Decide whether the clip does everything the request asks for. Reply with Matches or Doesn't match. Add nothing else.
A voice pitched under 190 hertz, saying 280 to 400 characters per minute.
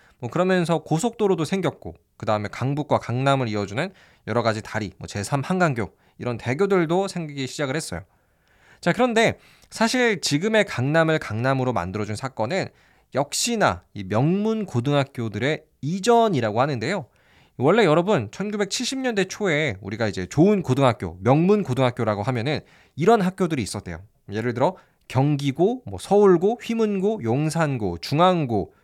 Matches